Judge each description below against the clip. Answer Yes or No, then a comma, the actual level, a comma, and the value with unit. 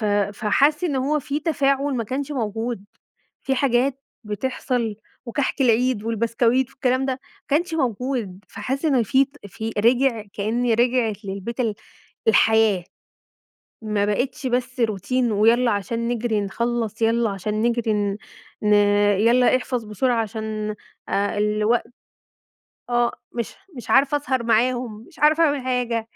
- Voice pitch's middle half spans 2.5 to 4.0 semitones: Yes, average, 3.2 semitones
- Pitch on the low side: No, high, 235 Hz